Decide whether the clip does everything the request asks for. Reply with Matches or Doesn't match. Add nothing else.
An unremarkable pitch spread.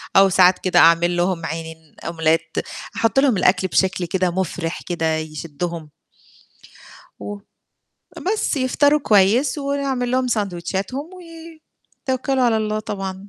Doesn't match